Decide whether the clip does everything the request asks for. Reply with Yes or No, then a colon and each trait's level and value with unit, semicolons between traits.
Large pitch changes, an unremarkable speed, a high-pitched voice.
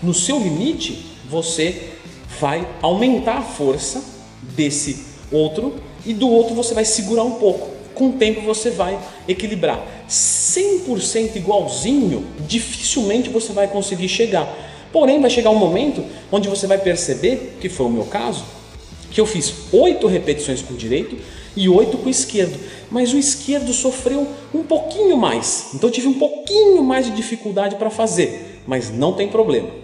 Yes: wide, 5.9 semitones; average, 160 wpm; high, 215 Hz